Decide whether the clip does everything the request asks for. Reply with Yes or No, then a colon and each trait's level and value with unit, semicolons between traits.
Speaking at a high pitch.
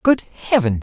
No: medium, 170 Hz